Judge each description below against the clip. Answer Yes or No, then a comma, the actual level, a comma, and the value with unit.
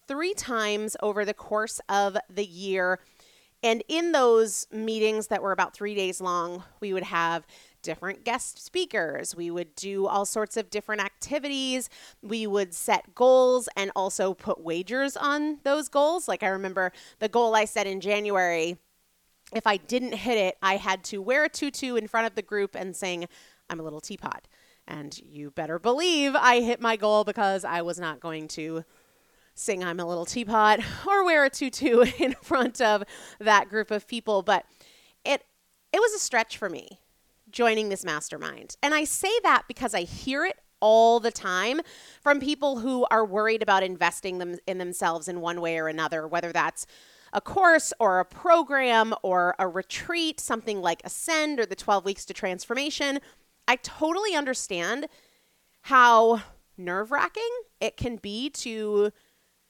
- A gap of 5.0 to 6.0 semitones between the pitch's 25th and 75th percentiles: Yes, average, 5.3 semitones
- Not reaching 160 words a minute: No, average, 170 wpm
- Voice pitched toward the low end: No, high, 215 Hz